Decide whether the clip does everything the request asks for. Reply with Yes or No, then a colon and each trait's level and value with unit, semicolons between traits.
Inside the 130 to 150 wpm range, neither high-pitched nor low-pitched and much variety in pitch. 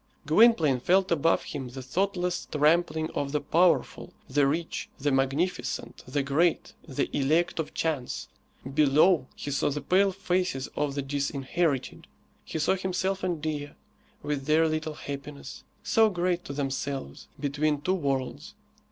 No: average, 145 wpm; medium, 150 Hz; average, 4.0 semitones